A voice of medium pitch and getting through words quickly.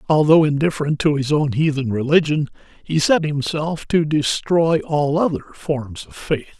No: medium, 150 Hz; average, 155 wpm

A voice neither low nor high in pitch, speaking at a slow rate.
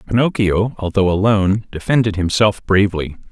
No: low, 100 Hz; slow, 110 wpm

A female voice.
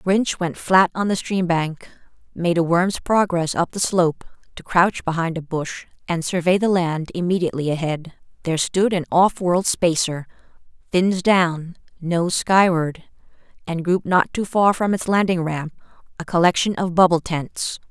Yes: female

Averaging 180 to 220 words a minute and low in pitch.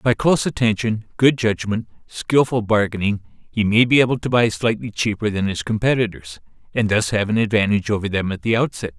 Yes: average, 185 wpm; low, 110 Hz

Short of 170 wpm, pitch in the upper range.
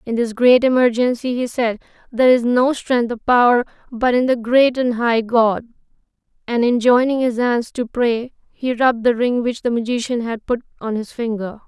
No: average, 195 wpm; high, 240 Hz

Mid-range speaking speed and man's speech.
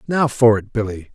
No: fast, 210 wpm; male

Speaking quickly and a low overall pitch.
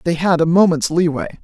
No: fast, 210 wpm; medium, 170 Hz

